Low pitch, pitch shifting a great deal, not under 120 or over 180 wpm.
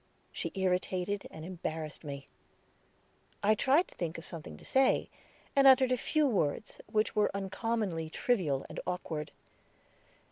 No: high, 190 Hz; wide, 6.4 semitones; average, 140 wpm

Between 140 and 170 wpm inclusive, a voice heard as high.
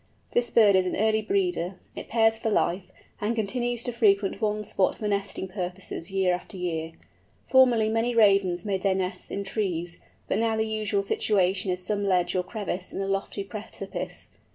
No: average, 180 wpm; high, 200 Hz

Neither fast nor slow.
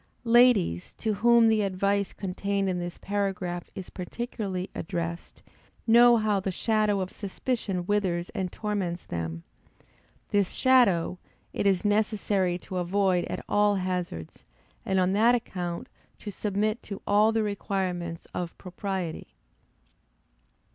No: slow, 125 wpm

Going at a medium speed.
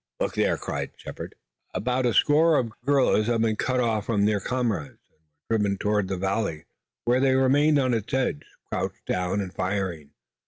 Yes: average, 190 wpm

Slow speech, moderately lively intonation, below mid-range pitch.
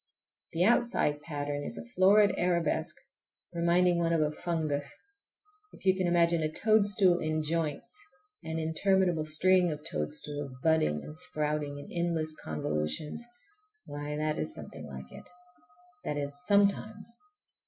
No: slow, 130 wpm; average, 4.1 semitones; medium, 165 Hz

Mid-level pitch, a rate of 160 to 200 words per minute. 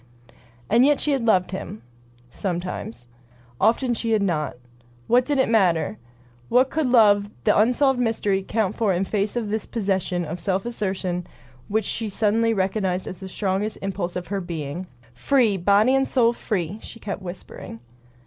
No: high, 205 Hz; average, 170 wpm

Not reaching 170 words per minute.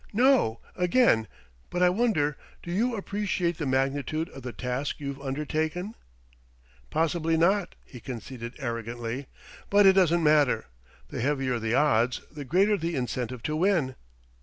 Yes: average, 140 wpm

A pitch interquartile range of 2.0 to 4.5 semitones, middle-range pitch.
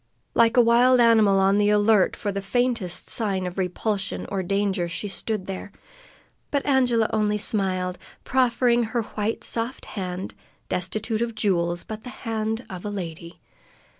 No: average, 3.4 semitones; high, 210 Hz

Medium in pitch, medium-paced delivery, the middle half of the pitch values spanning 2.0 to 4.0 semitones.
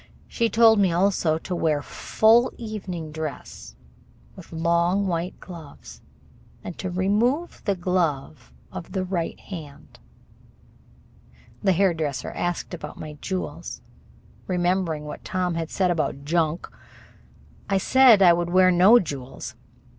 No: medium, 180 Hz; slow, 125 wpm; average, 3.1 semitones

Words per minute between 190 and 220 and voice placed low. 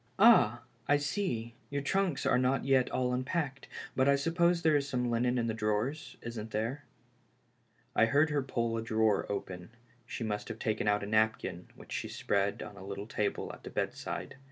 Yes: average, 200 wpm; low, 125 Hz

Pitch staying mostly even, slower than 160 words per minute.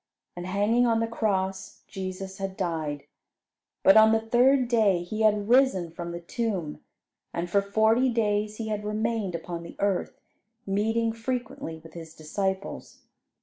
No: average, 3.7 semitones; average, 150 wpm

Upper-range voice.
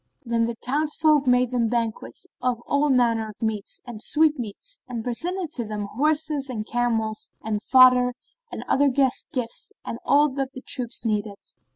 Yes: very high, 250 Hz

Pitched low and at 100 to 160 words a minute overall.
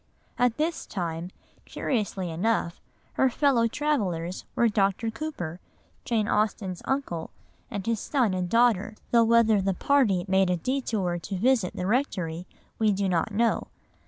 No: high, 210 Hz; average, 145 wpm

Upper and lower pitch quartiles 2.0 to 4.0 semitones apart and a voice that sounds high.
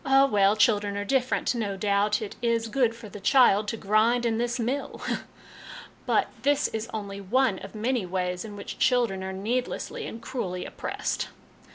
Yes: average, 3.5 semitones; high, 220 Hz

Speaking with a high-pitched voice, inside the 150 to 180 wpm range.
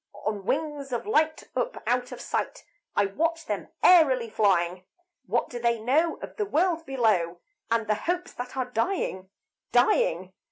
Yes: high, 245 Hz; average, 160 wpm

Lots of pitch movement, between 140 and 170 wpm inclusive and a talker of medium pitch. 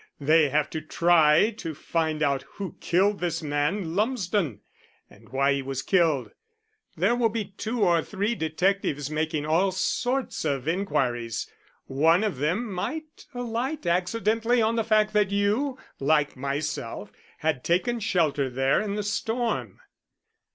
Yes: wide, 6.2 semitones; average, 145 wpm; medium, 175 Hz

